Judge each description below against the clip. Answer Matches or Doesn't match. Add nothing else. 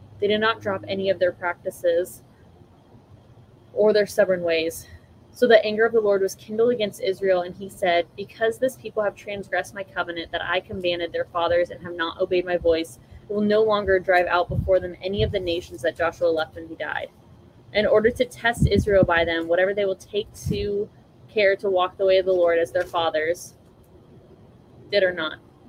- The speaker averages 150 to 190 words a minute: Doesn't match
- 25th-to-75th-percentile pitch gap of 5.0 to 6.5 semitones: Doesn't match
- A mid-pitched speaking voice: Matches